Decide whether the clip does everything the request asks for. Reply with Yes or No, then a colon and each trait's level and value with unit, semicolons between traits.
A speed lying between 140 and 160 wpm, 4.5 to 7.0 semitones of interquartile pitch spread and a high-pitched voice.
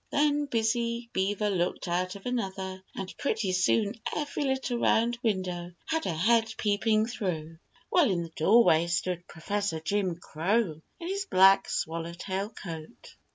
Yes: average, 145 wpm; average, 4.9 semitones; high, 200 Hz